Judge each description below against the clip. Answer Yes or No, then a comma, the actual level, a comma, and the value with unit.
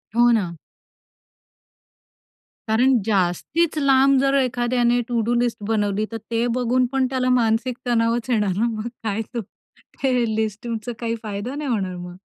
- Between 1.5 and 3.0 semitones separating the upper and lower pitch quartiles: Yes, narrow, 2.6 semitones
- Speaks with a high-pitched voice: Yes, high, 235 Hz